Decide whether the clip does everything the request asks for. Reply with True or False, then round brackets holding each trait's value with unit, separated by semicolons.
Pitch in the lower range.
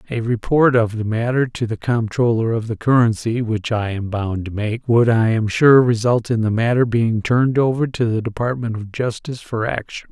True (115 Hz)